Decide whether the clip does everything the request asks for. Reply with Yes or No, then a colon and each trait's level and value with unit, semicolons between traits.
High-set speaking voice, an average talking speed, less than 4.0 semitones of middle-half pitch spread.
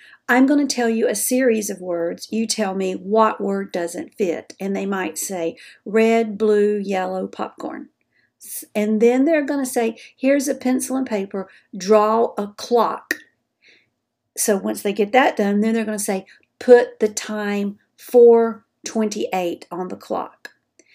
Yes: high, 215 Hz; average, 160 wpm; average, 3.2 semitones